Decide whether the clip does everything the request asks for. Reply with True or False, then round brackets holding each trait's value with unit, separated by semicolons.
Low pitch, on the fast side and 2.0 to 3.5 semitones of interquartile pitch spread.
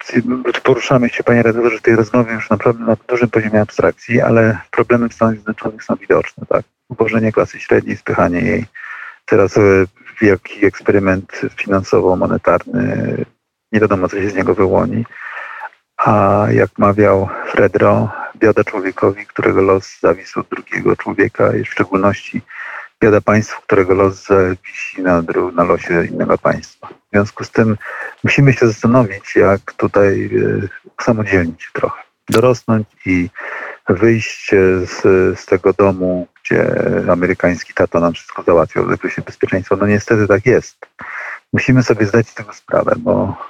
False (110 Hz; 140 wpm; 3.1 semitones)